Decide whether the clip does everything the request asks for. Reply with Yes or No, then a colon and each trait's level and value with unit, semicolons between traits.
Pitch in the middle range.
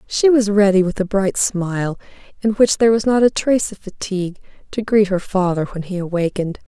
No: high, 195 Hz